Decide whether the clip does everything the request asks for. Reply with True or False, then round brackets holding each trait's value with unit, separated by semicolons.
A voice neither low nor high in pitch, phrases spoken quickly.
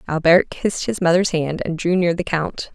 True (170 Hz; 220 wpm)